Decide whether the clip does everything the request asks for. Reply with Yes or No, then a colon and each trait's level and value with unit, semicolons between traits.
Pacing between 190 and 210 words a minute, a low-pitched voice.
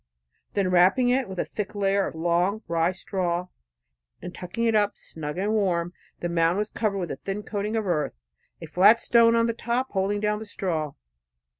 No: average, 200 wpm; high, 195 Hz